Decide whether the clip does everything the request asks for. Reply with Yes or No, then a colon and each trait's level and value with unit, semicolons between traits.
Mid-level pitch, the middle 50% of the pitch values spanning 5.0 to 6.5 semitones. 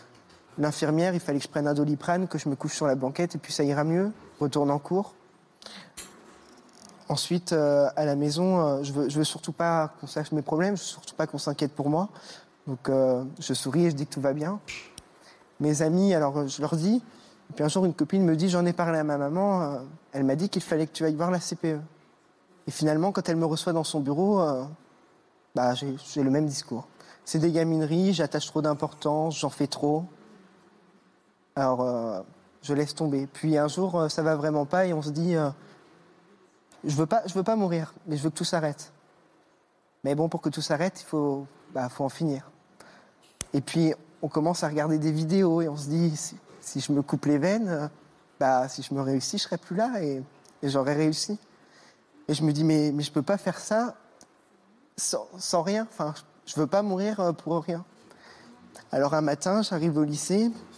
No: medium, 155 Hz; average, 3.2 semitones